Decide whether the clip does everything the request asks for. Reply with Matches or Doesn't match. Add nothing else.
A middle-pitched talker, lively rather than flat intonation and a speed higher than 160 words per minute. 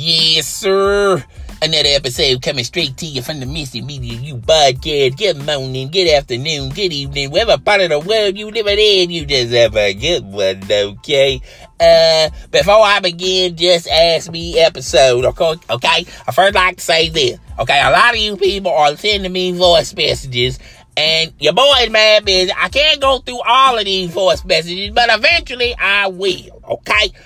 Matches